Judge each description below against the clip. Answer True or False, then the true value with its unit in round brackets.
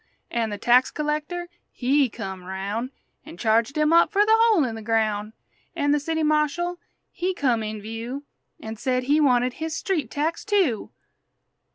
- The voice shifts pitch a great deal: True (6.1 semitones)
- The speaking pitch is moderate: False (270 Hz)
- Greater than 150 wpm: True (170 wpm)